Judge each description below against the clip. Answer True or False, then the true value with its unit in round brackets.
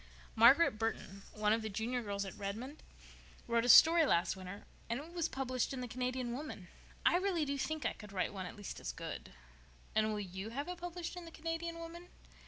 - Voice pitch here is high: True (250 Hz)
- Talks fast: True (210 wpm)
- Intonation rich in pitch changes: True (7.6 semitones)